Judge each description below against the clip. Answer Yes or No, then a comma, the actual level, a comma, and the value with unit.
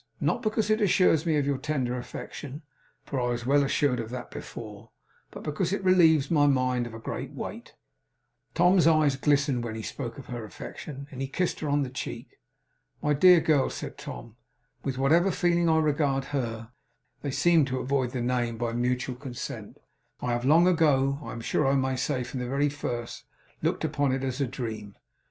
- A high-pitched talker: No, low, 135 Hz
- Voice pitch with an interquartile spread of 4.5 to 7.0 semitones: No, average, 3.7 semitones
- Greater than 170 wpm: Yes, average, 195 wpm